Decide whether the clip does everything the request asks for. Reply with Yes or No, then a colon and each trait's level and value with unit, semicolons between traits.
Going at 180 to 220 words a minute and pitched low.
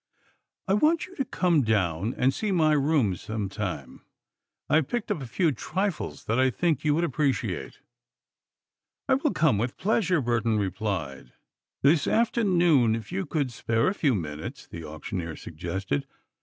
No: average, 155 wpm; low, 130 Hz